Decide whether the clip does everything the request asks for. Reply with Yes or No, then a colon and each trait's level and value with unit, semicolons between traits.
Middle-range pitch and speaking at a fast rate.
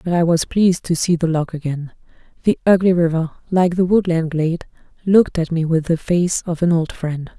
Yes: medium, 170 Hz; fast, 210 wpm